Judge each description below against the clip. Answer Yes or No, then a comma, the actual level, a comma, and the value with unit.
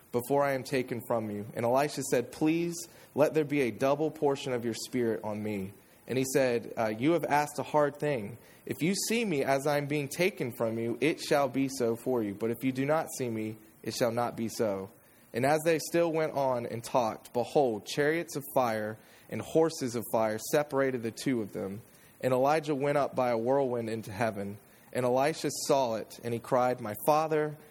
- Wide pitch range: No, average, 4.5 semitones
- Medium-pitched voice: No, low, 130 Hz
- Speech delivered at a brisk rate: Yes, fast, 215 wpm